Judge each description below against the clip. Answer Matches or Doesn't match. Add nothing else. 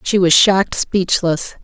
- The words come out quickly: Doesn't match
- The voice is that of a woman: Matches